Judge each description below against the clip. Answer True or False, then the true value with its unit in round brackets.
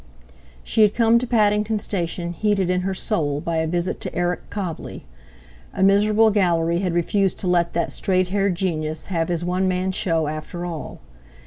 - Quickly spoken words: False (180 wpm)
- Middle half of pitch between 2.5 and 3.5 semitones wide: True (3.0 semitones)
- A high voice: False (180 Hz)